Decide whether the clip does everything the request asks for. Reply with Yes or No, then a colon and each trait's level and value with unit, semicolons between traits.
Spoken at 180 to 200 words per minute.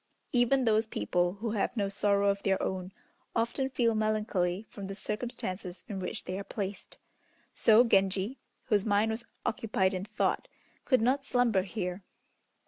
No: average, 155 wpm